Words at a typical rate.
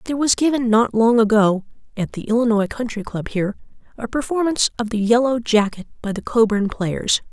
Yes: average, 180 wpm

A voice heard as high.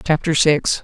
No: medium, 155 Hz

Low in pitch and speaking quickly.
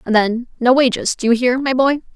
No: very high, 250 Hz; fast, 250 wpm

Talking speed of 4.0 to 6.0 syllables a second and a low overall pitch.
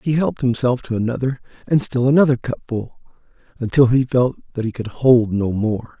Yes: 5.4 syllables/s; low, 125 Hz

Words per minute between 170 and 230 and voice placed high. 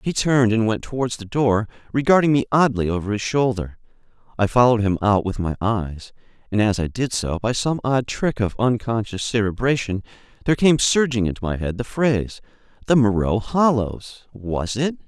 No: average, 175 wpm; low, 115 Hz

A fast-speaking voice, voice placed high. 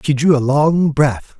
No: fast, 215 wpm; medium, 145 Hz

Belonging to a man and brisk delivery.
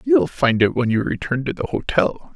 Yes: male; fast, 255 wpm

